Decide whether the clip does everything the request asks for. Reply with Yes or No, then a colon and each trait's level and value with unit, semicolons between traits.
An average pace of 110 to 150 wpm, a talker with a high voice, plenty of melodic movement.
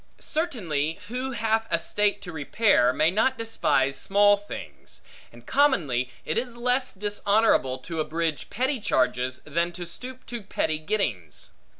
Yes: average, 140 wpm; high, 195 Hz; wide, 7.7 semitones